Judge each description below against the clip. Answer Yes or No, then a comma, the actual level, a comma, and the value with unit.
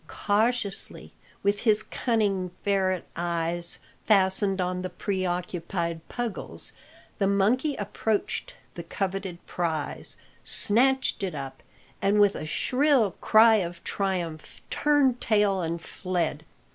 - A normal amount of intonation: Yes, average, 3.7 semitones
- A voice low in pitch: No, high, 195 Hz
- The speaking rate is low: Yes, slow, 110 wpm